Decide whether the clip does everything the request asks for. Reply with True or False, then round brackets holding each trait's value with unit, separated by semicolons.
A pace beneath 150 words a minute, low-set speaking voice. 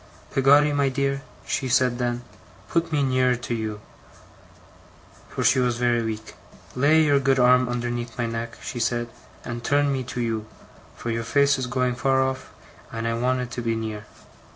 False (180 wpm; 125 Hz)